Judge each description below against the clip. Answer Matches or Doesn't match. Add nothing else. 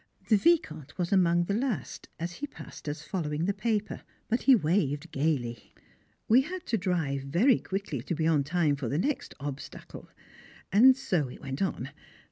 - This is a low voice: Doesn't match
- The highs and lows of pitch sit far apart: Matches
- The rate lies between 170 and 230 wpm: Matches